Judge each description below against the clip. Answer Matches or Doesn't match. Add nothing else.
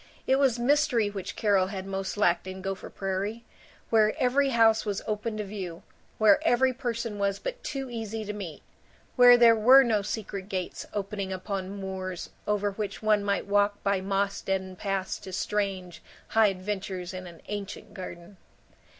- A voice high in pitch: Matches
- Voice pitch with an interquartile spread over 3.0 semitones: Doesn't match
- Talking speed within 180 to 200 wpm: Doesn't match